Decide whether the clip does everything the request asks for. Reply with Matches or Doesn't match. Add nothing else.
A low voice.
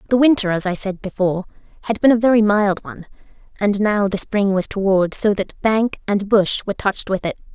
Doesn't match